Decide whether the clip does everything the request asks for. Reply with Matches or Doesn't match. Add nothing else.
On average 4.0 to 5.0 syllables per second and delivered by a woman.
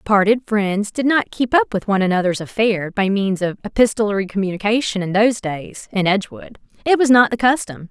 Doesn't match